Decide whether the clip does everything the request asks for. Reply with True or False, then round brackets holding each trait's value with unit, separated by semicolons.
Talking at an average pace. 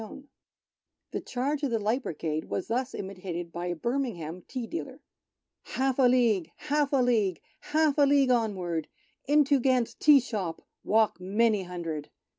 True (165 wpm)